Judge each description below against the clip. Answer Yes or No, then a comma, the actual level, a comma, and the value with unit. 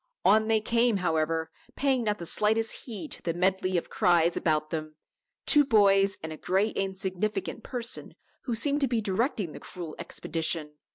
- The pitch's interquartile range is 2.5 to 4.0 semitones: No, average, 5.0 semitones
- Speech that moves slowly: No, average, 170 wpm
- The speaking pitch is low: No, high, 195 Hz